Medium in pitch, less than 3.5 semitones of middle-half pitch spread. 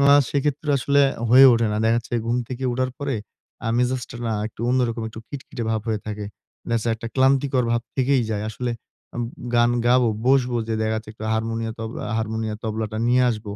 No: low, 120 Hz; narrow, 2.6 semitones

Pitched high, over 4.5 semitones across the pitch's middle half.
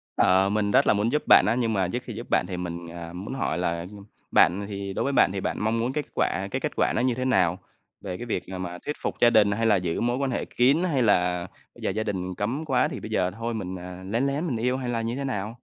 No: low, 105 Hz; average, 4.9 semitones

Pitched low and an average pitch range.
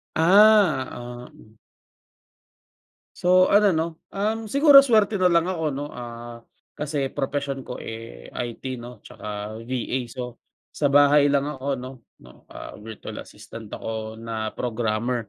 No: low, 130 Hz; wide, 6.1 semitones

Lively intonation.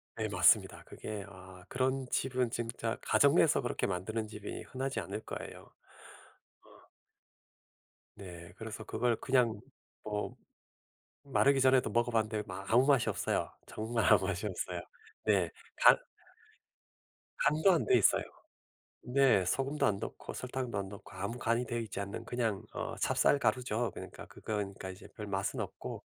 No: average, 4.0 semitones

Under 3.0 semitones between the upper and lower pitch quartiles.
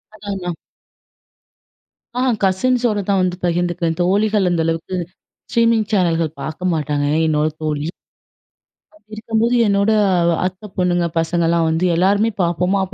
No: average, 3.7 semitones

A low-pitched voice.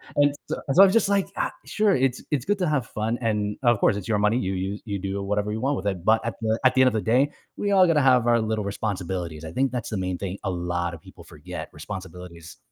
Yes: low, 110 Hz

